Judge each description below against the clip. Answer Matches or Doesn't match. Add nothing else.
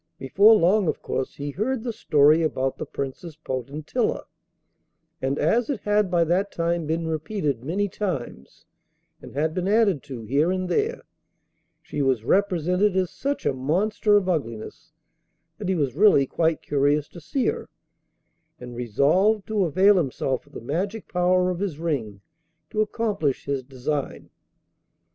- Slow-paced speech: Doesn't match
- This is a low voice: Doesn't match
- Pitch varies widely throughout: Matches